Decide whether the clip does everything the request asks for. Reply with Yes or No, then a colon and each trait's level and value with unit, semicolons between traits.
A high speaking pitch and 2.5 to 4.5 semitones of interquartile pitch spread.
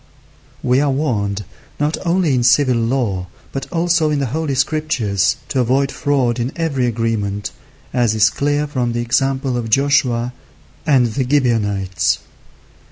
No: low, 125 Hz; average, 3.8 semitones